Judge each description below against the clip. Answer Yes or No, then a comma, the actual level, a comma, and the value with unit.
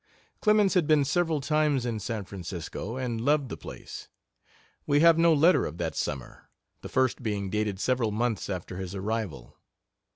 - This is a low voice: Yes, low, 115 Hz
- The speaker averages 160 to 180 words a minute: Yes, average, 165 wpm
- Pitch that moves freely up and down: Yes, wide, 7.2 semitones